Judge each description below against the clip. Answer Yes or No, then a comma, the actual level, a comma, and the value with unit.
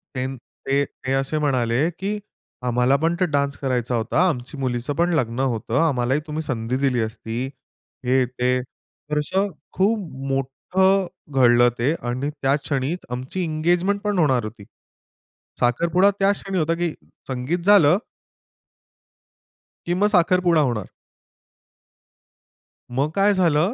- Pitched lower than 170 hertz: Yes, medium, 140 Hz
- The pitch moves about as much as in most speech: No, wide, 5.8 semitones